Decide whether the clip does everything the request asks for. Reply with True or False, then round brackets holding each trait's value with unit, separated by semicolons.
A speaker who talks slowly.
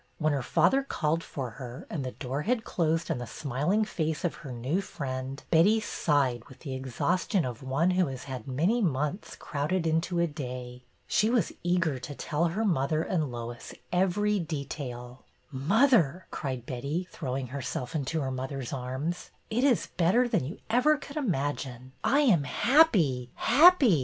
False (170 wpm)